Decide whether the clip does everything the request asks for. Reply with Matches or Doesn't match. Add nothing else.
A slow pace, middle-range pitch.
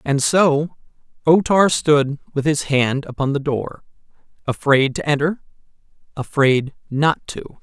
Matches